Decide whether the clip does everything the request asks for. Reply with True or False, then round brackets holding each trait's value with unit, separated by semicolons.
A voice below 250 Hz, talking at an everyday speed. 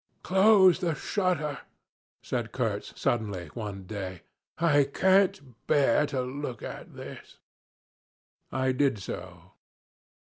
False (135 Hz; 105 wpm)